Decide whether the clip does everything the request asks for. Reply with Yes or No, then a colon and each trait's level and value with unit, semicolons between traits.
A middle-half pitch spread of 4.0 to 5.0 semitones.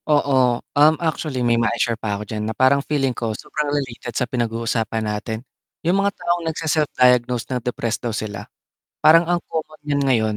Yes: average, 4.6 semitones